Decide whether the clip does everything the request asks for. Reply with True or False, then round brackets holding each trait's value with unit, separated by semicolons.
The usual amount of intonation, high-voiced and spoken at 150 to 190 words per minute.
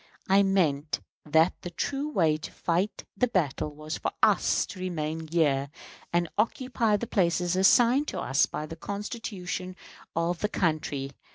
False (4.6 semitones; 175 Hz; 155 wpm)